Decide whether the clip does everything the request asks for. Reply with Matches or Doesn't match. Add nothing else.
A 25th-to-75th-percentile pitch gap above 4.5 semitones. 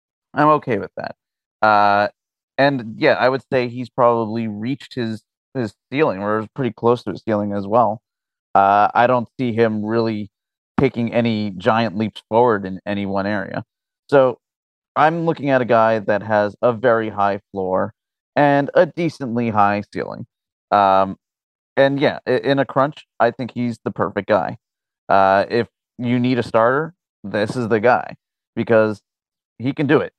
Doesn't match